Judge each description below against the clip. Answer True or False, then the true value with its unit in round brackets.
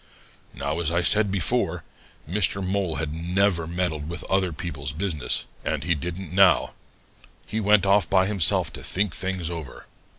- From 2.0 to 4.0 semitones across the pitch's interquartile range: True (3.1 semitones)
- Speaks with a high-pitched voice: False (90 Hz)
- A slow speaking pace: False (160 wpm)